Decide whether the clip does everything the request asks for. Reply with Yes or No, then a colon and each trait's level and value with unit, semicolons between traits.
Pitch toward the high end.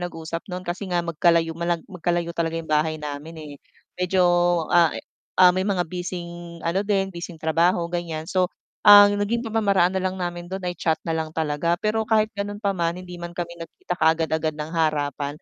No: medium, 175 Hz